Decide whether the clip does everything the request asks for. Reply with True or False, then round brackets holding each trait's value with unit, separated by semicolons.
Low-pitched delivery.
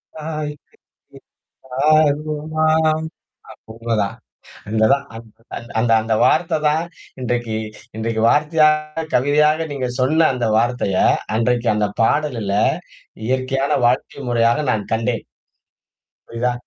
True (130 Hz)